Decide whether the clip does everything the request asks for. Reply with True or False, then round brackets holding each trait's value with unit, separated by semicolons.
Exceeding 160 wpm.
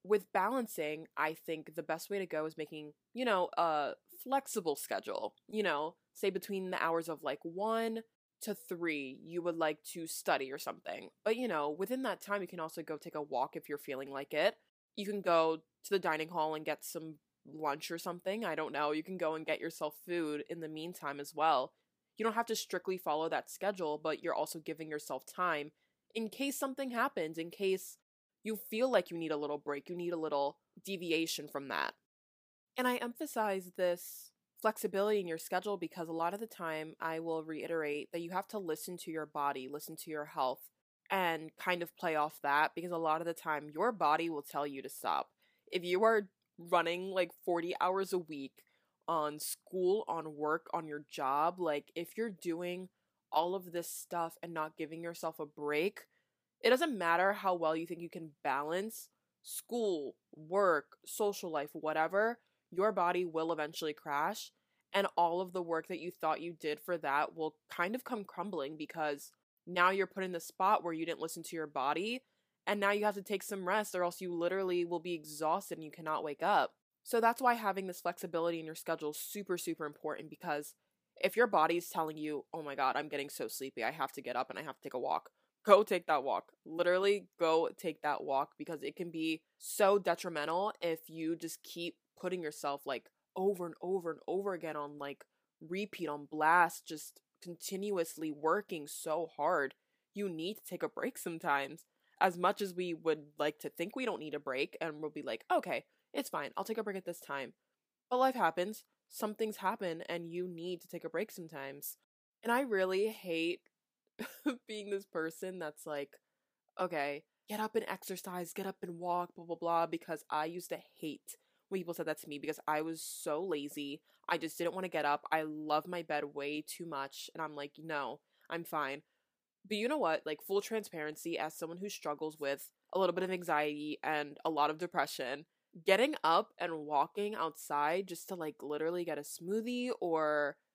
True (205 wpm)